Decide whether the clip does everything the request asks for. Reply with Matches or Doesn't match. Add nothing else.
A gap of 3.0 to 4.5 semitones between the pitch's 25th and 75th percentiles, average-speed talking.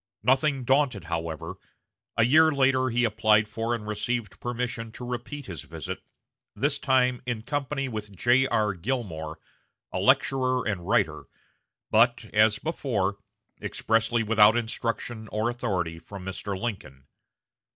Doesn't match